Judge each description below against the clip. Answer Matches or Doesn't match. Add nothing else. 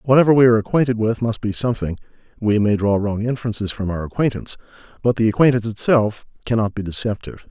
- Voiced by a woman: Doesn't match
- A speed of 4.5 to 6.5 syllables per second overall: Doesn't match